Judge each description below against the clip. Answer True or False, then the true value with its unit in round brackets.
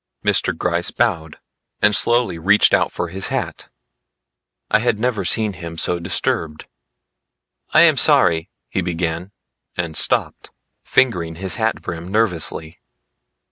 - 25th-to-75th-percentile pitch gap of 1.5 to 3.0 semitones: False (4.1 semitones)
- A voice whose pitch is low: True (90 Hz)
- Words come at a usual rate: False (130 wpm)